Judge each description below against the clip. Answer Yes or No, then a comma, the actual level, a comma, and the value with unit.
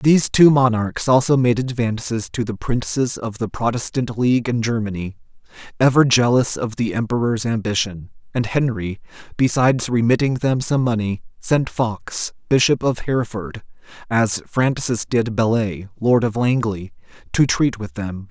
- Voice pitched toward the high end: No, low, 120 Hz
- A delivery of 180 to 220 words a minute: No, average, 145 wpm